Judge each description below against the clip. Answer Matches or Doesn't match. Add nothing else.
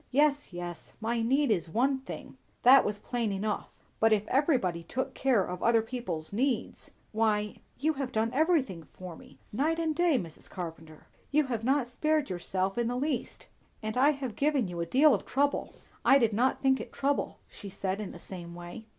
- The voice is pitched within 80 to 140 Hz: Doesn't match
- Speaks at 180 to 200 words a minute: Matches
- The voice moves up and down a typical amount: Doesn't match